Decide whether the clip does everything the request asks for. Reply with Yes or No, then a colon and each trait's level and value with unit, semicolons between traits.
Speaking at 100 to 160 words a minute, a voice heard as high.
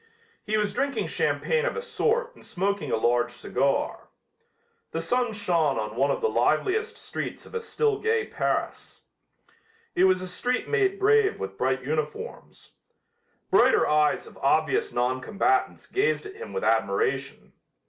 Yes: average, 155 wpm; high, 215 Hz